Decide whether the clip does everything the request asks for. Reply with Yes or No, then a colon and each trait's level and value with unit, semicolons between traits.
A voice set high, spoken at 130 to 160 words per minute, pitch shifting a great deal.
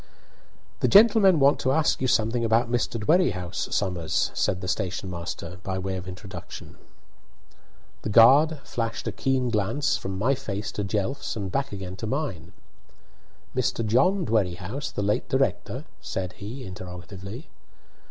No: low, 105 Hz; average, 145 wpm; wide, 5.7 semitones